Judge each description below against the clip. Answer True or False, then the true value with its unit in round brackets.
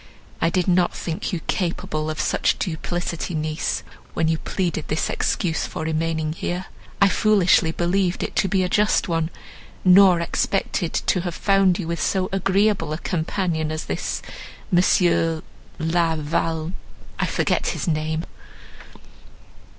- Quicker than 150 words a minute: False (145 wpm)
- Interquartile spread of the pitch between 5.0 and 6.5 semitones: False (2.6 semitones)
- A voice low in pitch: False (170 Hz)